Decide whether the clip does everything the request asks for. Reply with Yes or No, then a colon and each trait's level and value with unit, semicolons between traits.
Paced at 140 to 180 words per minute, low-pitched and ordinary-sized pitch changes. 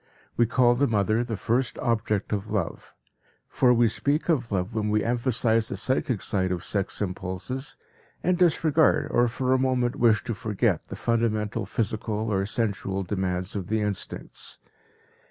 Yes: average, 160 wpm; low, 110 Hz; average, 3.4 semitones